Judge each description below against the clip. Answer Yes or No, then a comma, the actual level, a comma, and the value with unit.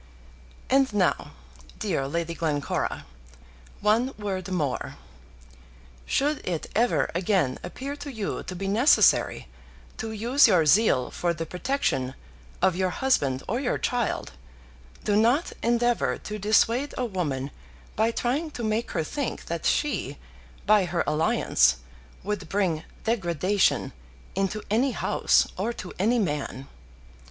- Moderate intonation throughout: No, wide, 6.0 semitones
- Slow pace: Yes, slow, 130 wpm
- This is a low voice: No, high, 205 Hz